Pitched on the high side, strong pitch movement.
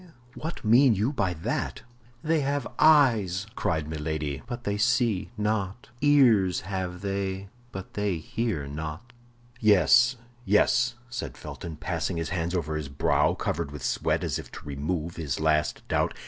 No: very low, 95 Hz; wide, 7.0 semitones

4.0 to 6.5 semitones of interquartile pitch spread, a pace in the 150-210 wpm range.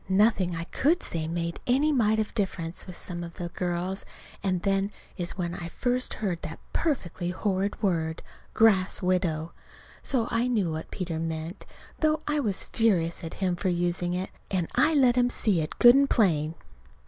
Yes: average, 4.7 semitones; average, 180 wpm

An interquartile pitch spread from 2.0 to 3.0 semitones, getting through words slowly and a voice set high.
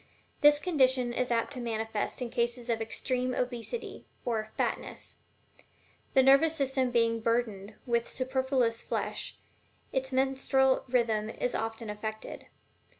Yes: narrow, 2.5 semitones; slow, 130 wpm; high, 245 Hz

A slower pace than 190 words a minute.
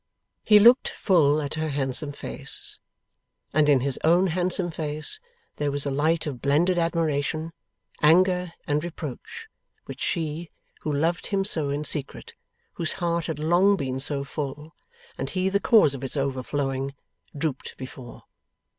Yes: average, 150 wpm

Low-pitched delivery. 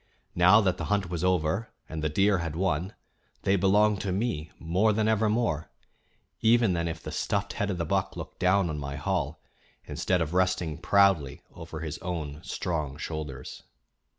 Yes: very low, 90 Hz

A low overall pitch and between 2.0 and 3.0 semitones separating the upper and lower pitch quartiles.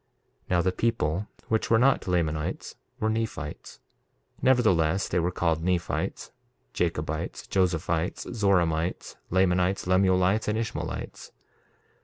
No: very low, 90 Hz; average, 3.9 semitones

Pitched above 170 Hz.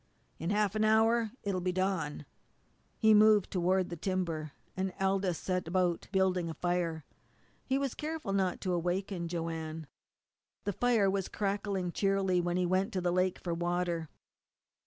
Yes: medium, 185 Hz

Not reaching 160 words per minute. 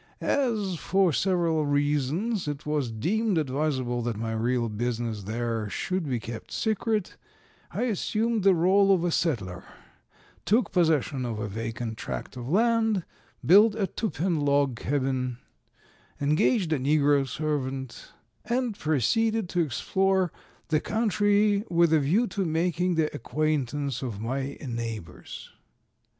Yes: slow, 135 wpm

